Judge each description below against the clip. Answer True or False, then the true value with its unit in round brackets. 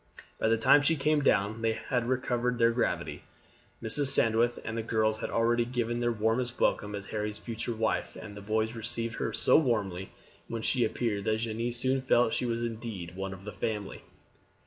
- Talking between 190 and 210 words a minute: True (200 wpm)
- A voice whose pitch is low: True (115 Hz)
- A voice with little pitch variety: True (1.8 semitones)